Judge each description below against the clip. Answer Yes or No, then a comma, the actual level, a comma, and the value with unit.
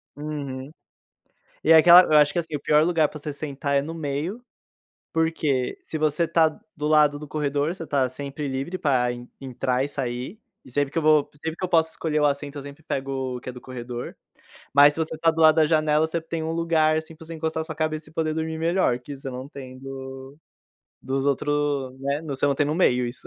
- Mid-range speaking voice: Yes, medium, 150 Hz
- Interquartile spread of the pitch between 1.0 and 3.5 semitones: Yes, average, 2.8 semitones